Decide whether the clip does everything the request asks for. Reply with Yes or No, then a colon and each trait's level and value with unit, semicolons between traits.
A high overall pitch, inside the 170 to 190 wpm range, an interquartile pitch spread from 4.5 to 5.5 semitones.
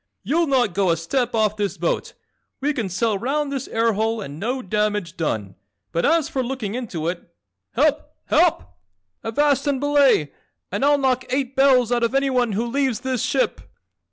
Yes: high, 240 Hz; average, 180 wpm; average, 5.0 semitones